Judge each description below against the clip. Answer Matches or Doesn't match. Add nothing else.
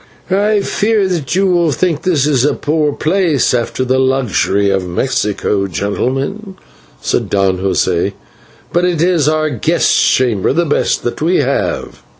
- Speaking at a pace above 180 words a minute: Doesn't match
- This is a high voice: Doesn't match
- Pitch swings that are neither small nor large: Doesn't match